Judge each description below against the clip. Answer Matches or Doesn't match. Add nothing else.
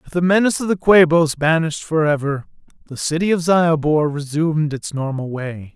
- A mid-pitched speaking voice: Matches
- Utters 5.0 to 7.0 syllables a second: Matches